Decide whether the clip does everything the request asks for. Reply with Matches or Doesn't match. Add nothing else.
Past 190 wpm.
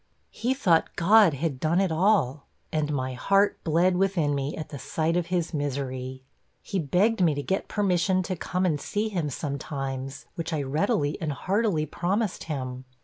Doesn't match